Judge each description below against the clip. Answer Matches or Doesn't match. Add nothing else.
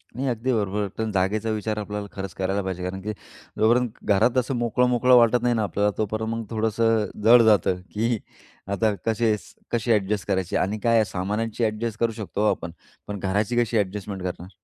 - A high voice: Doesn't match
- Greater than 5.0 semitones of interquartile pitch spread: Doesn't match